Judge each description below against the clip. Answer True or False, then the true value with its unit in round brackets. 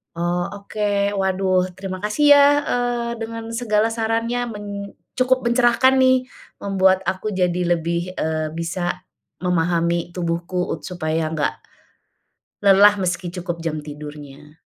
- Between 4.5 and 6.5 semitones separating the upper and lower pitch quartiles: True (4.8 semitones)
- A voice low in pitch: False (185 Hz)